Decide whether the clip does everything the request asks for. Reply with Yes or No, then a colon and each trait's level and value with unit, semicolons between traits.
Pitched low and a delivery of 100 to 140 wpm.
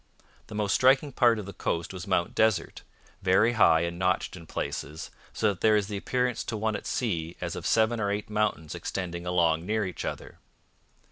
No: low, 100 Hz; average, 200 wpm